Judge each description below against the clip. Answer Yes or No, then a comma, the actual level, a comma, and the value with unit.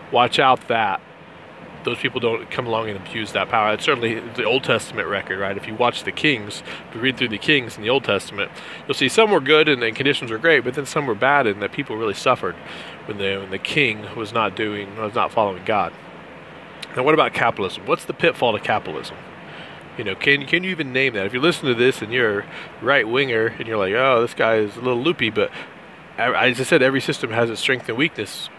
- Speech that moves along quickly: Yes, fast, 235 wpm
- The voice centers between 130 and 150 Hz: No, low, 120 Hz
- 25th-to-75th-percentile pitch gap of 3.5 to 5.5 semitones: Yes, average, 4.0 semitones